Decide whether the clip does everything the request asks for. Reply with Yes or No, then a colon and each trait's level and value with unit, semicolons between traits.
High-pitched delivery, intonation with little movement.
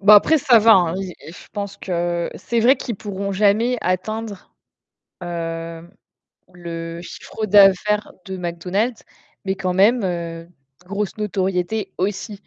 No: high, 195 Hz; average, 3.2 semitones